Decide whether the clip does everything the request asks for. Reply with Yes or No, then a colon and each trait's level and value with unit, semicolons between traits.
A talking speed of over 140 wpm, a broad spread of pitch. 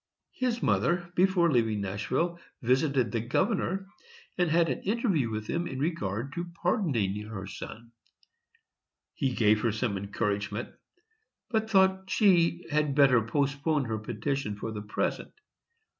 No: slow, 135 wpm; wide, 8.0 semitones